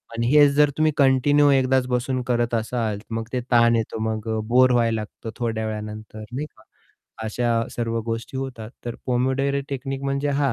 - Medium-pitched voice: No, low, 120 Hz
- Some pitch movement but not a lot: Yes, average, 3.0 semitones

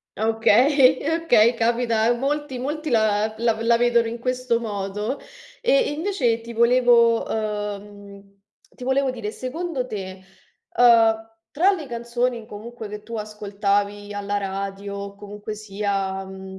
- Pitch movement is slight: No, average, 3.4 semitones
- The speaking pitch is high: Yes, high, 225 Hz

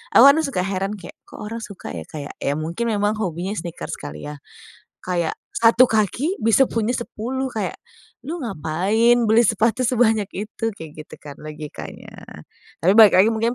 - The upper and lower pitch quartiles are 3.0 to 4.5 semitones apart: No, average, 5.2 semitones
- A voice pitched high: Yes, high, 210 Hz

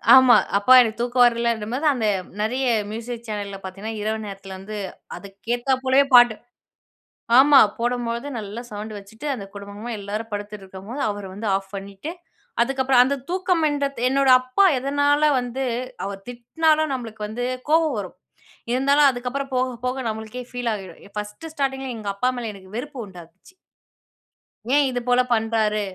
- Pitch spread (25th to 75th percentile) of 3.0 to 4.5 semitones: Yes, average, 4.1 semitones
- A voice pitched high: Yes, high, 235 Hz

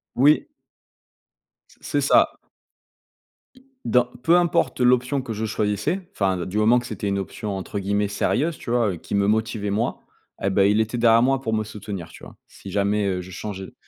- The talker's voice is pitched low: Yes, low, 105 Hz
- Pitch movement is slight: No, average, 3.6 semitones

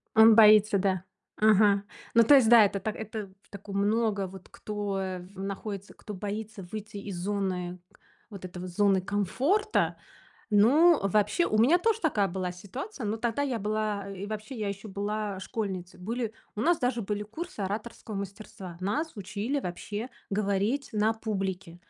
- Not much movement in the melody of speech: Yes, narrow, 2.3 semitones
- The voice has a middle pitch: No, high, 210 Hz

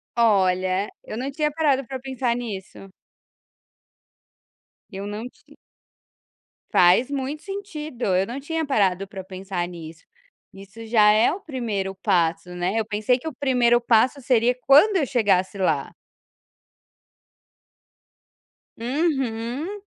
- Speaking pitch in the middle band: No, high, 230 Hz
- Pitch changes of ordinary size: No, wide, 6.0 semitones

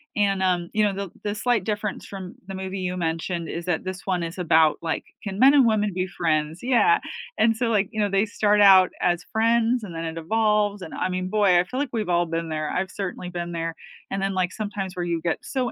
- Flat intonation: No, average, 3.3 semitones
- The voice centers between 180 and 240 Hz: Yes, high, 190 Hz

